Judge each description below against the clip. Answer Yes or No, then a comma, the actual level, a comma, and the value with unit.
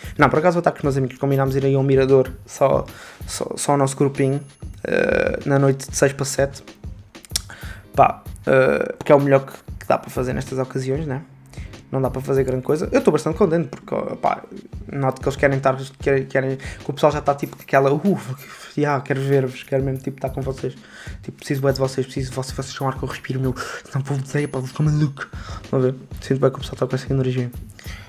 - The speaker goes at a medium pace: No, fast, 235 wpm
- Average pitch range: No, narrow, 1.3 semitones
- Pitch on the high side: No, low, 135 Hz